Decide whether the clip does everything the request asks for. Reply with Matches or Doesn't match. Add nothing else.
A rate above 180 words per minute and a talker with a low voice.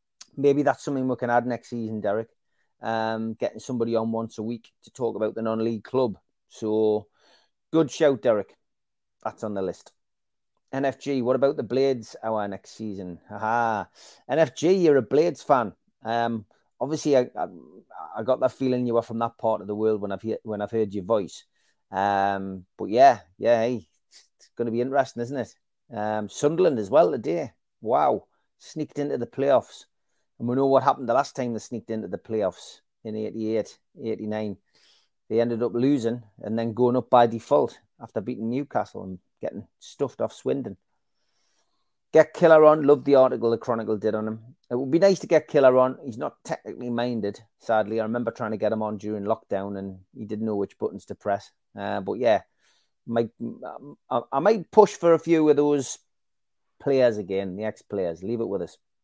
Matches